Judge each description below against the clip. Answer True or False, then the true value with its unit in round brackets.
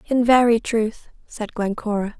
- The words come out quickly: False (135 wpm)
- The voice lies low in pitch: False (225 Hz)